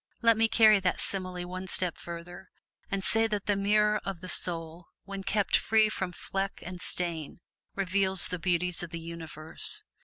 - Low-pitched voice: No, medium, 185 Hz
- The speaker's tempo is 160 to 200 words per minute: Yes, average, 175 wpm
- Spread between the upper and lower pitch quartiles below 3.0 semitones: Yes, narrow, 2.4 semitones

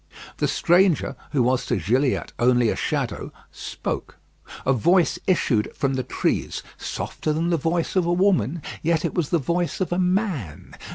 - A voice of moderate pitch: Yes, medium, 160 Hz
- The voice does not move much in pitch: No, wide, 5.5 semitones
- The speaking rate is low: No, average, 170 wpm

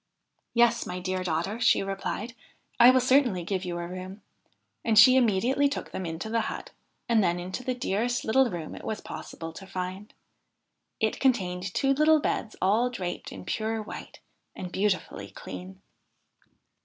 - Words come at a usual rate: Yes, average, 170 wpm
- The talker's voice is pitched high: Yes, high, 205 Hz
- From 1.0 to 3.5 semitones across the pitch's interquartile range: No, average, 4.9 semitones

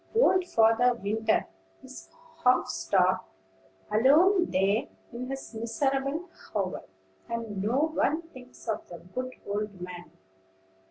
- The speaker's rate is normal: No, slow, 115 wpm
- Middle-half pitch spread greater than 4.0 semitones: Yes, average, 4.8 semitones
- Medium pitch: No, high, 235 Hz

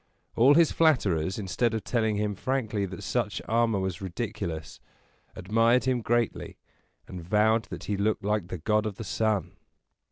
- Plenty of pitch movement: No, average, 3.4 semitones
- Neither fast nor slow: Yes, average, 160 wpm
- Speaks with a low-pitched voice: Yes, low, 105 Hz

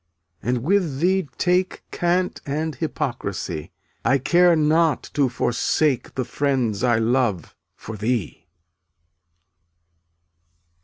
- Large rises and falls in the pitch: Yes, wide, 5.8 semitones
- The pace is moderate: No, slow, 100 wpm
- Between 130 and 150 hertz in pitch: Yes, medium, 140 Hz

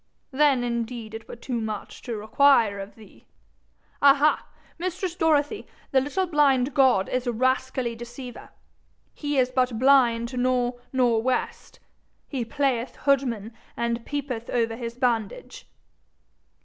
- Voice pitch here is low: No, very high, 250 Hz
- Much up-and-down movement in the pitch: No, average, 3.0 semitones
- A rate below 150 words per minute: Yes, slow, 135 wpm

